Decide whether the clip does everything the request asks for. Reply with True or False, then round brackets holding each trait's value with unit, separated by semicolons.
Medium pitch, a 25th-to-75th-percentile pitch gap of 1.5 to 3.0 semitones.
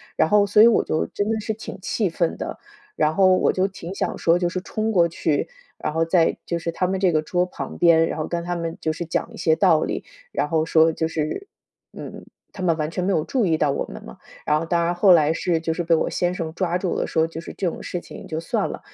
True (170 Hz; 2.4 semitones)